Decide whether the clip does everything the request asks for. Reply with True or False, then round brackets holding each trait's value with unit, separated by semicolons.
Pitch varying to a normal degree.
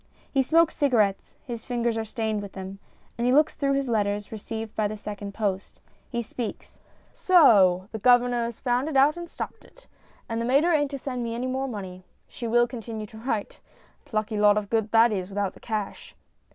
True (3.5 semitones)